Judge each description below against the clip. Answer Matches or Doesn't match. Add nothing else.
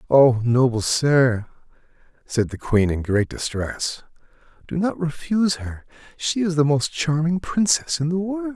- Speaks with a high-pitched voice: Doesn't match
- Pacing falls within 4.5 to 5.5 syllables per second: Doesn't match